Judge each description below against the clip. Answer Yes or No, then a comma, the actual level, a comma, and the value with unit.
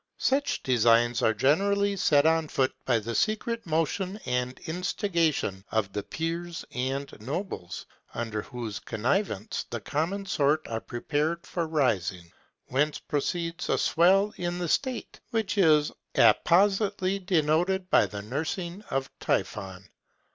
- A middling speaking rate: No, slow, 130 wpm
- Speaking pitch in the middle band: Yes, medium, 155 Hz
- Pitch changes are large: Yes, wide, 7.2 semitones